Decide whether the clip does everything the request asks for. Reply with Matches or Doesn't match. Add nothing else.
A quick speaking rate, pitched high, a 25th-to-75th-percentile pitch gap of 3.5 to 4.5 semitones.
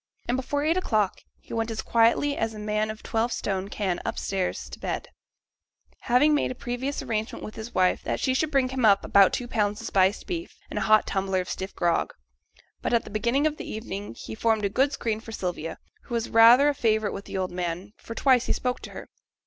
Matches